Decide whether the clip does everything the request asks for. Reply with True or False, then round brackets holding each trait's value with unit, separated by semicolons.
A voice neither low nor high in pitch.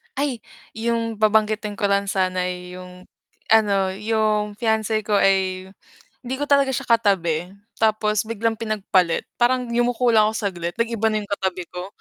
False (215 Hz)